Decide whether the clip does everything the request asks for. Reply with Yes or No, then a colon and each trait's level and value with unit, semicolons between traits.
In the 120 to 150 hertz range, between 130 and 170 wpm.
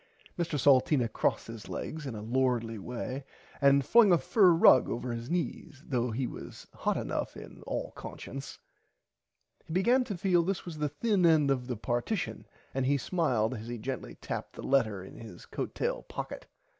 No: low, 135 Hz; average, 180 wpm